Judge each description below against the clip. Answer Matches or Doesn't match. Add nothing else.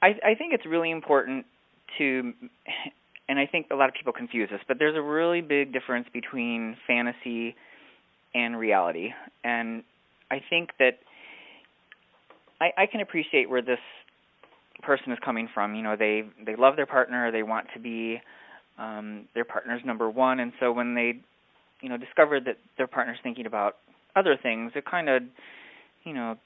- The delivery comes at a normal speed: Matches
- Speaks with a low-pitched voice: Matches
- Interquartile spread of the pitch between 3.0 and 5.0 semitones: Matches